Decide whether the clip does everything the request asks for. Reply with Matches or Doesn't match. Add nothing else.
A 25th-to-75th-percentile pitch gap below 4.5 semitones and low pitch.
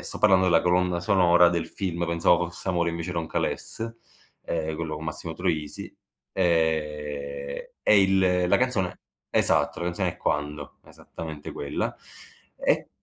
Matches